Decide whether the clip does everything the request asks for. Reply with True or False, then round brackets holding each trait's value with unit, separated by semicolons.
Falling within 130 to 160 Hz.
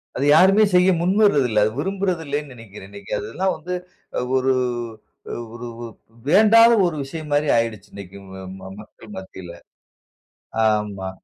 True (135 Hz)